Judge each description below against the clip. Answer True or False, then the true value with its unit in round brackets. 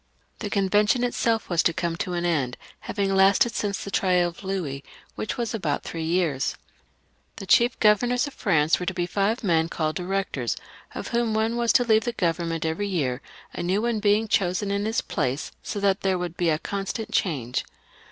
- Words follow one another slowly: False (205 wpm)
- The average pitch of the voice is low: False (195 Hz)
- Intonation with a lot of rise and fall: False (4.2 semitones)